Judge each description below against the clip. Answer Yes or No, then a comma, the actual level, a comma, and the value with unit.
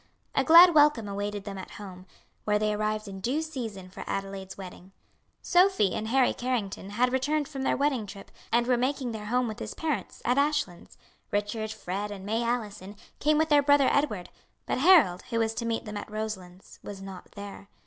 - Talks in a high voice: Yes, high, 220 Hz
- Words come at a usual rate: Yes, average, 195 wpm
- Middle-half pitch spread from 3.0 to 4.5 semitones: No, average, 5.0 semitones